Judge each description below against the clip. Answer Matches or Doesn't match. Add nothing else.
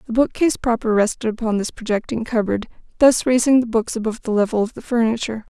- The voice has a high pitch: Matches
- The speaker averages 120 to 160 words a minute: Doesn't match